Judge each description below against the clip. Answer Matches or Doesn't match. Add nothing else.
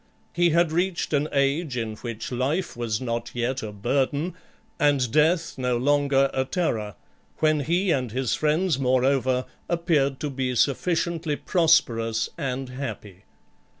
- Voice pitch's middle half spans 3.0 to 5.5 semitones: Matches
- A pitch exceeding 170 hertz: Doesn't match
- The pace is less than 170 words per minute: Matches